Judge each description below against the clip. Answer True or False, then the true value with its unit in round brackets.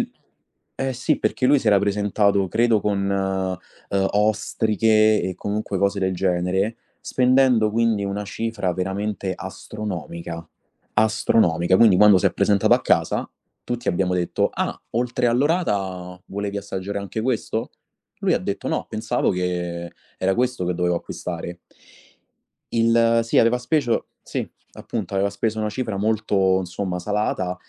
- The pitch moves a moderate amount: True (3.2 semitones)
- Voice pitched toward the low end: True (100 Hz)